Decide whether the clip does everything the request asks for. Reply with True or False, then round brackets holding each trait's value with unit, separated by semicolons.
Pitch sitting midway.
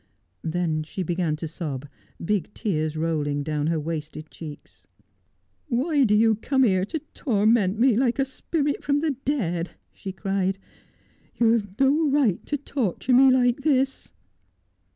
False (210 Hz)